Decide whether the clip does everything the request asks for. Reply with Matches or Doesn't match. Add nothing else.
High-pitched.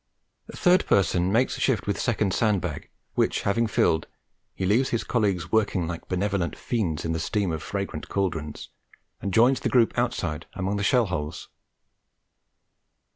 Doesn't match